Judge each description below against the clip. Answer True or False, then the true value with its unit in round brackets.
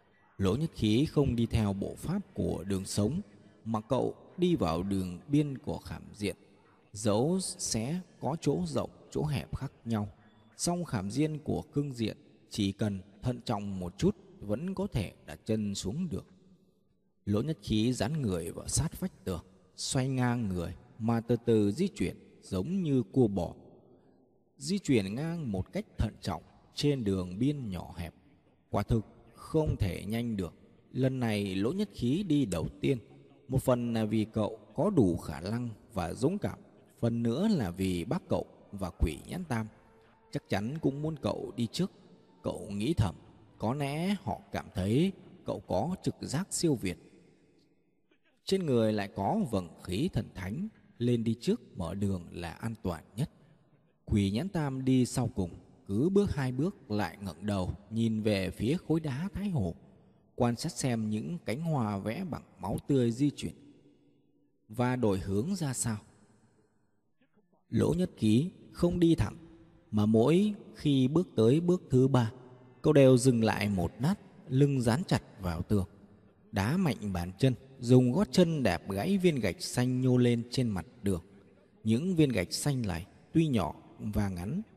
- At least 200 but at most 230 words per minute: False (170 wpm)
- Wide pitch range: True (7.0 semitones)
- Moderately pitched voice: False (115 Hz)